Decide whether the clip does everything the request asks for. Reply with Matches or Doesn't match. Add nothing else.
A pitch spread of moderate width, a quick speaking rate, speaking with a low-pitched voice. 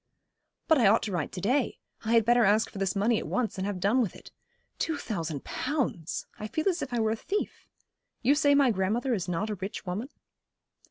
Doesn't match